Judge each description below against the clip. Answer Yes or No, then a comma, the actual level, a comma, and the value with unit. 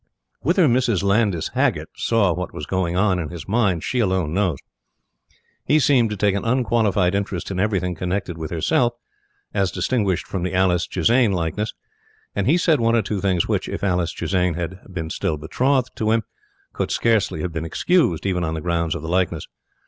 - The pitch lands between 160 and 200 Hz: No, very low, 95 Hz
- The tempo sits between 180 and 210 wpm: Yes, average, 190 wpm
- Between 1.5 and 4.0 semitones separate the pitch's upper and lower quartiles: No, average, 4.4 semitones